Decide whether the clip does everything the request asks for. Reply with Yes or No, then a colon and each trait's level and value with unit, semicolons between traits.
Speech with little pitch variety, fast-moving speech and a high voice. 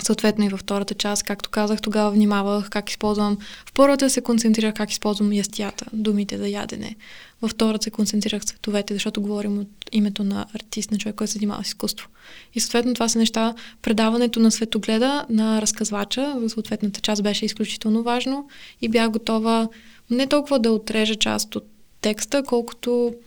Yes: narrow, 1.7 semitones; fast, 170 wpm; high, 215 Hz